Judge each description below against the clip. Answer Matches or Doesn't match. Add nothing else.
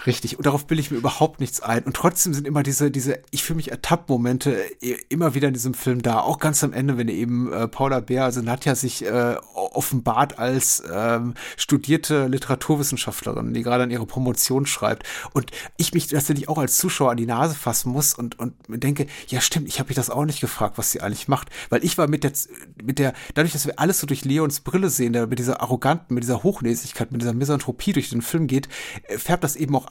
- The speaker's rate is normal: Doesn't match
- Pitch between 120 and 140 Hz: Matches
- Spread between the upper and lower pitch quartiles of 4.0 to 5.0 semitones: Doesn't match